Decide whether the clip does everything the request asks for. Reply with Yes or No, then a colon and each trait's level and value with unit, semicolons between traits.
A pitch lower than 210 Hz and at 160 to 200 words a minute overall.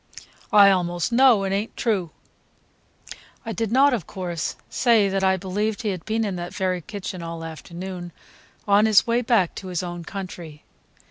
Yes: high, 190 Hz; average, 180 wpm